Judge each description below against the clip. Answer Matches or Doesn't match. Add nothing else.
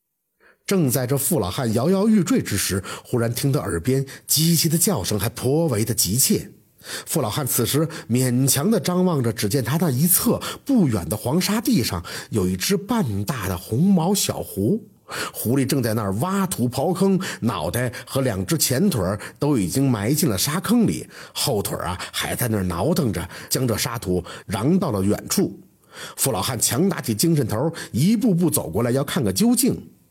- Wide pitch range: Matches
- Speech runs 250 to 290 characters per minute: Matches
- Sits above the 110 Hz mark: Matches